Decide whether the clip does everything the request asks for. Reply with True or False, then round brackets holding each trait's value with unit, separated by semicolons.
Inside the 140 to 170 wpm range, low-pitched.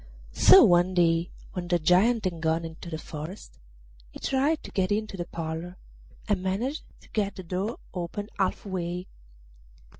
False (160 wpm; 180 Hz)